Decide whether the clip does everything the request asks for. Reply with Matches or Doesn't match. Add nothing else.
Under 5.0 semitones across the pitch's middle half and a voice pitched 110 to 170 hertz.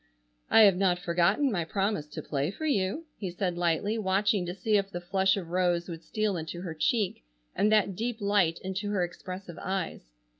Doesn't match